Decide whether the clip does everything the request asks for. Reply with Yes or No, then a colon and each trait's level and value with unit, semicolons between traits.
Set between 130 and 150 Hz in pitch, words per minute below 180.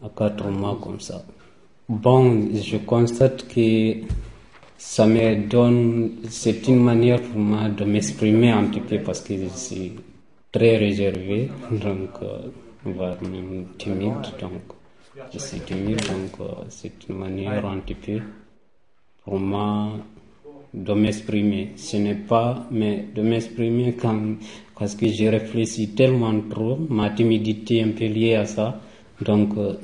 No: low, 110 Hz; slow, 145 wpm